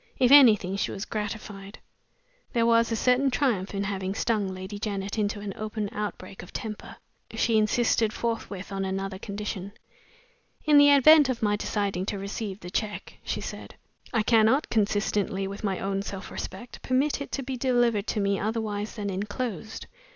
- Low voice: No, high, 210 Hz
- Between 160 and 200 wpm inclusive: Yes, average, 170 wpm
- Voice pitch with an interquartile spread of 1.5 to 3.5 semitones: Yes, average, 2.8 semitones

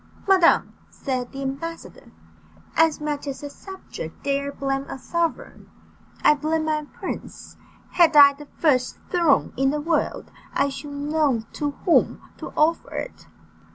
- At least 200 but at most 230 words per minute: No, average, 145 wpm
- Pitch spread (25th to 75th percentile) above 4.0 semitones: No, narrow, 2.6 semitones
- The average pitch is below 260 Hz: No, very high, 295 Hz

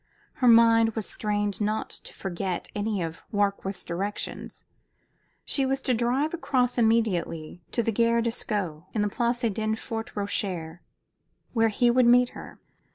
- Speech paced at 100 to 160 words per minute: Yes, average, 150 wpm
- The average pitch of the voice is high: Yes, high, 220 Hz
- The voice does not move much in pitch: No, average, 3.0 semitones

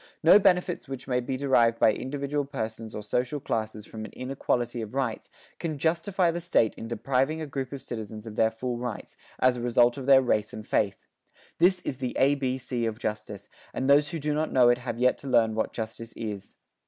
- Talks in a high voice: No, low, 125 Hz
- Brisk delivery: Yes, fast, 215 wpm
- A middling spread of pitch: Yes, average, 3.9 semitones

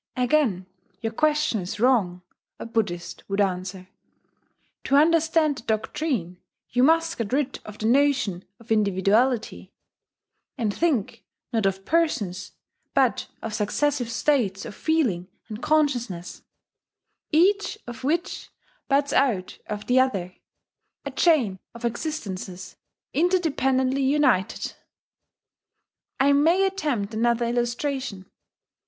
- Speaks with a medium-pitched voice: No, high, 245 Hz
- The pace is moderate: No, slow, 110 wpm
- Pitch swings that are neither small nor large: No, wide, 6.4 semitones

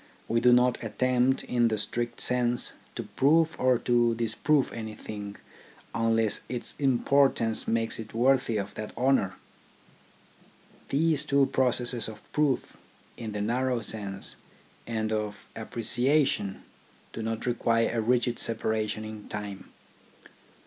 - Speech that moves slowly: Yes, slow, 125 wpm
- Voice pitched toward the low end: Yes, low, 115 Hz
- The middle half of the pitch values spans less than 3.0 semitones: Yes, narrow, 2.6 semitones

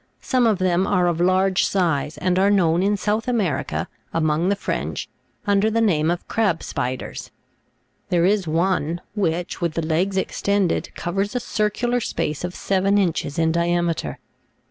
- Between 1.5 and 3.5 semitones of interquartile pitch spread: Yes, average, 3.2 semitones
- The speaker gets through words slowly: No, average, 160 wpm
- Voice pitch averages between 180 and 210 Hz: Yes, medium, 185 Hz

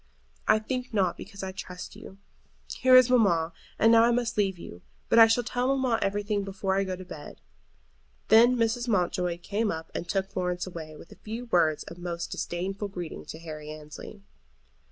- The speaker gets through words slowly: No, average, 190 wpm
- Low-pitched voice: No, high, 195 Hz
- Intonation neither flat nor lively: Yes, average, 4.5 semitones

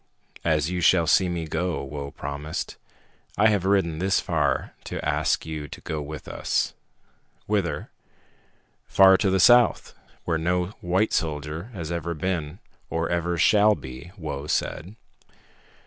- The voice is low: Yes, very low, 85 Hz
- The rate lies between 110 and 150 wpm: Yes, average, 145 wpm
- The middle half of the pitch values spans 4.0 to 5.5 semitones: No, average, 3.4 semitones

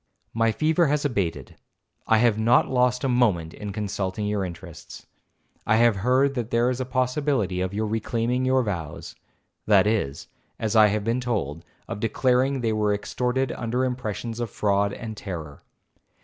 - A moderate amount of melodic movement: Yes, average, 3.7 semitones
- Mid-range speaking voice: No, low, 115 Hz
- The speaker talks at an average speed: Yes, average, 155 wpm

